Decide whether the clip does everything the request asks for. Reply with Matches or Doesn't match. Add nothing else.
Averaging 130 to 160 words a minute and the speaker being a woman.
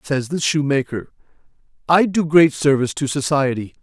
Doesn't match